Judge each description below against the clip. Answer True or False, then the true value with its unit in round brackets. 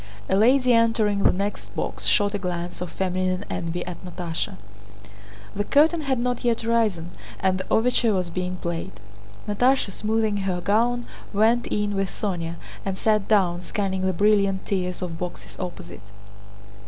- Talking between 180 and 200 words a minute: False (155 wpm)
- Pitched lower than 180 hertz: False (195 Hz)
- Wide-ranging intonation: False (3.5 semitones)